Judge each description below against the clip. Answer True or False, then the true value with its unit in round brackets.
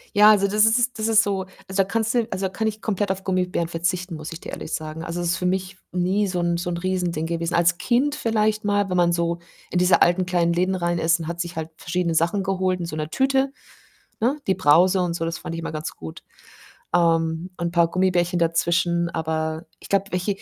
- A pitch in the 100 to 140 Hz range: False (180 Hz)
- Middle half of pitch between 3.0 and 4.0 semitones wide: False (2.5 semitones)